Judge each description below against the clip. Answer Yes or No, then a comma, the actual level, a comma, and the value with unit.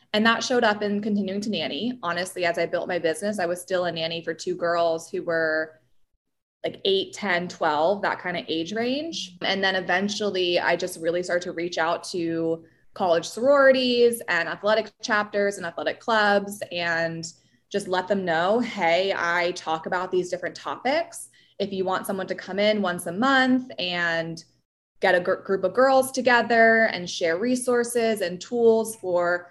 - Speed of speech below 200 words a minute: Yes, average, 175 wpm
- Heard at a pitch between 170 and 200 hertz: Yes, medium, 185 Hz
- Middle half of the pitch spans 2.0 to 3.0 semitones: No, average, 4.3 semitones